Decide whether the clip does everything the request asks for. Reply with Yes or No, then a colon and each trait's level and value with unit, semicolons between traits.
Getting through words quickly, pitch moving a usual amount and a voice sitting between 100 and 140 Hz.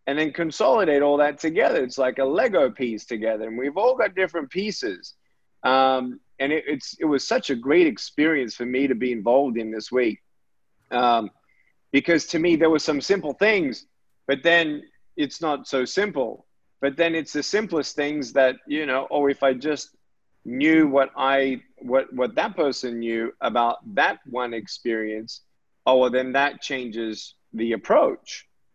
No: average, 175 wpm; average, 3.7 semitones; low, 135 Hz